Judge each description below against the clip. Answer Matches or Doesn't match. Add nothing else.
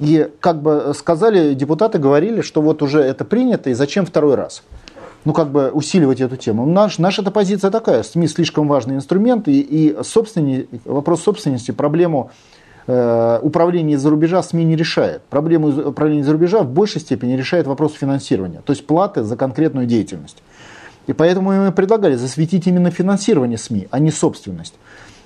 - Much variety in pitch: Doesn't match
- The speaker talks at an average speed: Doesn't match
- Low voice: Doesn't match